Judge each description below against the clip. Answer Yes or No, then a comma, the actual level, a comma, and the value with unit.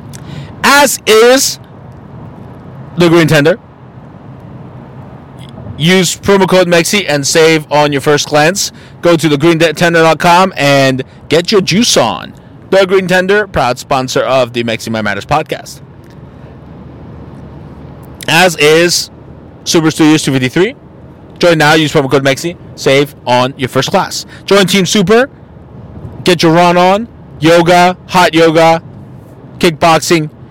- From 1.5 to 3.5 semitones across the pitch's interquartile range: No, average, 4.6 semitones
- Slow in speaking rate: Yes, slow, 120 wpm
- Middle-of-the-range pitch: Yes, medium, 160 Hz